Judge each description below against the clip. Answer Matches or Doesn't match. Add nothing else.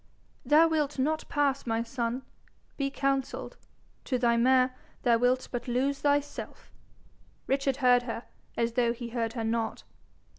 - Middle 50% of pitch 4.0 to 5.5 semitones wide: Doesn't match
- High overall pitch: Matches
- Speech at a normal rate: Matches